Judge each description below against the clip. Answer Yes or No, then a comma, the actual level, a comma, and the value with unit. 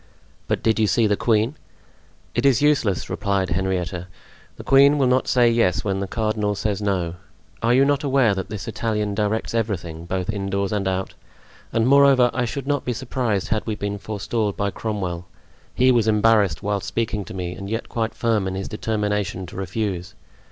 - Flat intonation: No, average, 3.2 semitones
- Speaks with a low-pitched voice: Yes, low, 105 Hz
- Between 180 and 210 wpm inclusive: Yes, average, 185 wpm